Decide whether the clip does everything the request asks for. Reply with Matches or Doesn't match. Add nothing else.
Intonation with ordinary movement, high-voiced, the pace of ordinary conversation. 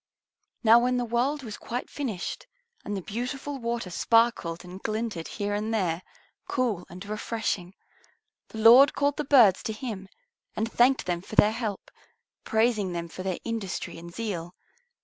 Matches